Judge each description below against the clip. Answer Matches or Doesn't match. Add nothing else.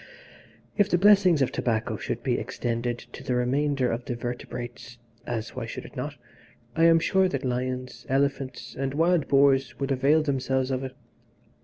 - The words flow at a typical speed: Matches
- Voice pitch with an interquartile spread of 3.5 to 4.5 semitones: Doesn't match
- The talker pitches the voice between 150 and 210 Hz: Doesn't match